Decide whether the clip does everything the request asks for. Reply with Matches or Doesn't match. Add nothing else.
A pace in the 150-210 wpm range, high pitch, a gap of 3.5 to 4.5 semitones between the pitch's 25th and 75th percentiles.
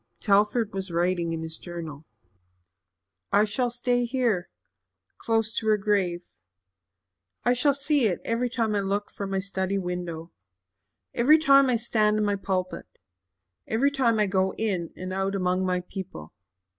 Matches